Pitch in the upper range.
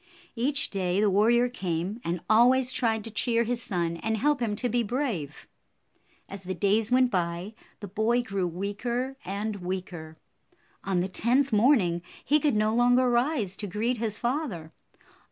Yes: high, 215 Hz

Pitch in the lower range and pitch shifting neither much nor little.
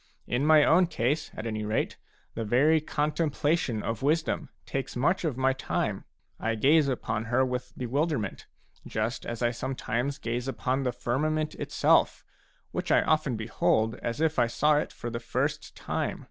Yes: low, 130 Hz; average, 4.4 semitones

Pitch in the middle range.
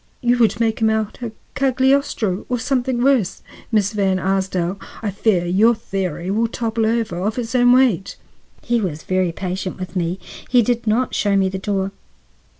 No: high, 215 Hz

